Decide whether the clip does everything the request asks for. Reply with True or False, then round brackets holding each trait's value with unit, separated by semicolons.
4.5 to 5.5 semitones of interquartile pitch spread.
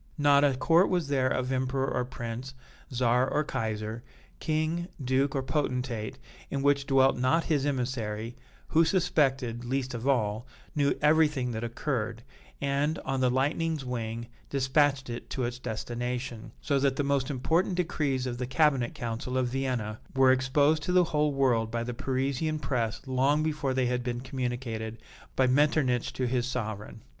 False (2.8 semitones)